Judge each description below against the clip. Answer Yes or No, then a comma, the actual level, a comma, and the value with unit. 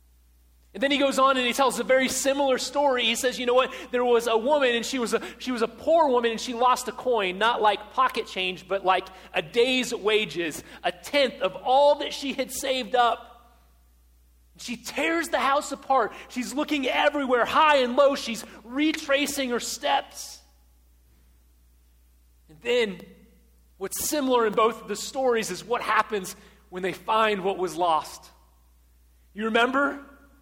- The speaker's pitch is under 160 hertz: No, high, 235 Hz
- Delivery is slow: No, average, 175 wpm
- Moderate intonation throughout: No, wide, 6.1 semitones